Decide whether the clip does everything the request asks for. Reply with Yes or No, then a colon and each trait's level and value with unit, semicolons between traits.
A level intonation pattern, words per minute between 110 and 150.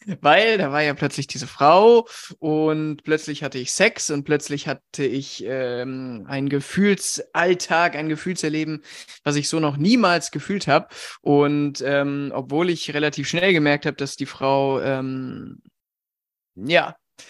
No: average, 3.0 semitones; average, 140 wpm